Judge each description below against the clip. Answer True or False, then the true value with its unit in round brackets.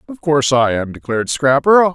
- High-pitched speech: False (145 Hz)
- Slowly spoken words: False (185 wpm)